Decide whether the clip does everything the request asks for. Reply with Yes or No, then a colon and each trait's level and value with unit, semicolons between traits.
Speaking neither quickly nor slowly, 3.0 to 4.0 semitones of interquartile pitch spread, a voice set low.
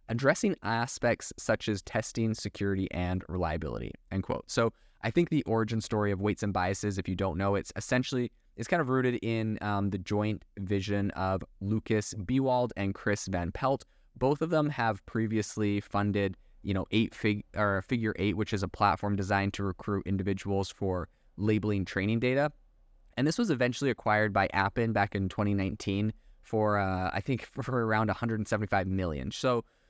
No: average, 175 wpm; narrow, 2.5 semitones; low, 105 Hz